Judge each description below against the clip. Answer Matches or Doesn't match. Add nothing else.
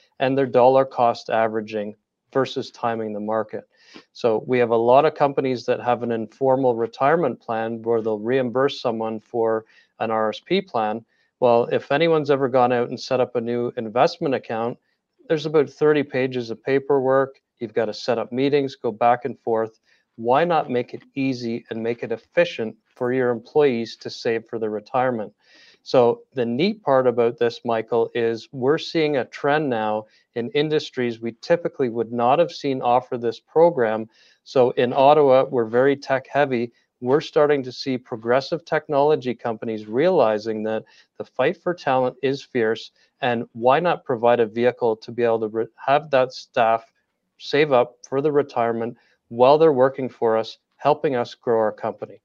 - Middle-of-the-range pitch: Doesn't match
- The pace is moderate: Matches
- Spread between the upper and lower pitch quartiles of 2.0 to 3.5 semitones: Matches